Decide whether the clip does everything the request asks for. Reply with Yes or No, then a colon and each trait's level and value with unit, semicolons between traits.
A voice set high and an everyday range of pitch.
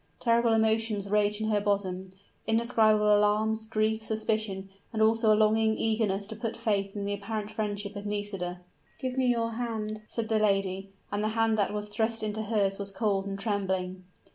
No: high, 215 Hz; narrow, 1.6 semitones